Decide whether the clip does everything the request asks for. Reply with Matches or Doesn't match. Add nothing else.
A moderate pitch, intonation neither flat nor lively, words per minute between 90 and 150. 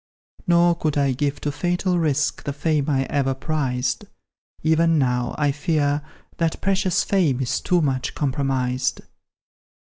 Matches